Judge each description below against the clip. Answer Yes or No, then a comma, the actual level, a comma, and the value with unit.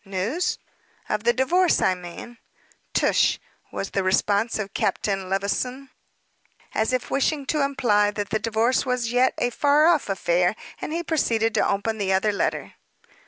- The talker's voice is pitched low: No, high, 225 Hz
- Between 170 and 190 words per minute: No, average, 160 wpm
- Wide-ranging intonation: No, average, 4.8 semitones